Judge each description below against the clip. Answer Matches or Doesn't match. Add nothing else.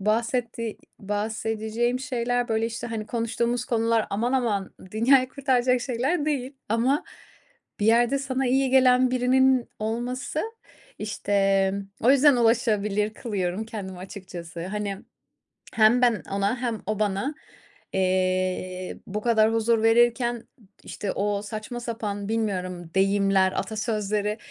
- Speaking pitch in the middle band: Doesn't match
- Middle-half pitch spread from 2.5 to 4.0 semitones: Matches